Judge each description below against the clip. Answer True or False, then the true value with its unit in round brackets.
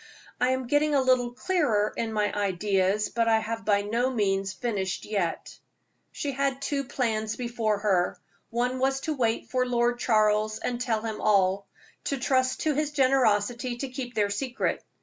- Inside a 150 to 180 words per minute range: True (170 wpm)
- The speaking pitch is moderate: False (235 Hz)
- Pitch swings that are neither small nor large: True (3.6 semitones)